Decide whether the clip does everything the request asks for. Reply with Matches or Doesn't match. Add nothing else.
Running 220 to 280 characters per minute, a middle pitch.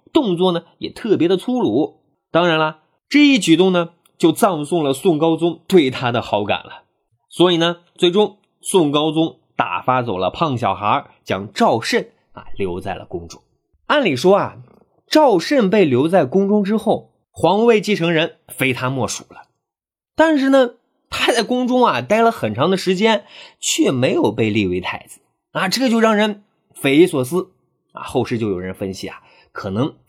Matches